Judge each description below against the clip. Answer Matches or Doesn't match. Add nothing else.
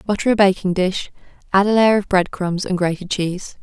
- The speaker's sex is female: Matches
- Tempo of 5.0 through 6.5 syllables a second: Matches